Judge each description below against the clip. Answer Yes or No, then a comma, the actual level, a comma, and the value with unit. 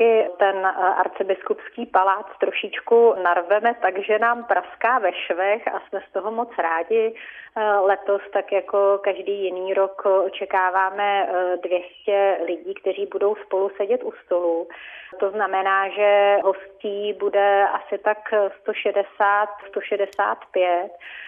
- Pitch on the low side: No, high, 200 Hz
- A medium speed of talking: No, slow, 110 wpm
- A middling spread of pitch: No, narrow, 1.4 semitones